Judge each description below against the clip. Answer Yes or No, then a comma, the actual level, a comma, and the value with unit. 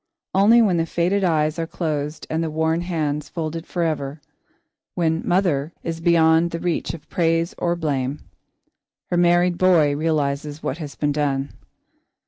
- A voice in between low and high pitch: Yes, medium, 165 Hz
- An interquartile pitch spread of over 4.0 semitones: No, narrow, 2.4 semitones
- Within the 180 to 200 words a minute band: No, average, 150 wpm